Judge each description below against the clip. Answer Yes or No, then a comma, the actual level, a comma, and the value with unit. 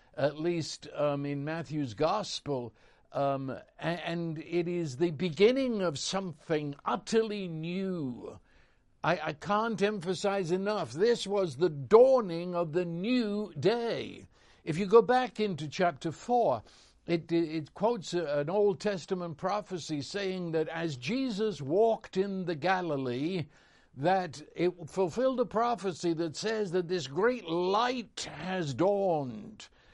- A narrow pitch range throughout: No, average, 4.5 semitones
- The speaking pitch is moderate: Yes, medium, 180 Hz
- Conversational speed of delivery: No, slow, 130 wpm